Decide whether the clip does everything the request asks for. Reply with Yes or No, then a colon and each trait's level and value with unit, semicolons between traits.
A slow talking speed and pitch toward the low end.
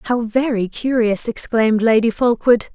No: slow, 130 wpm; high, 230 Hz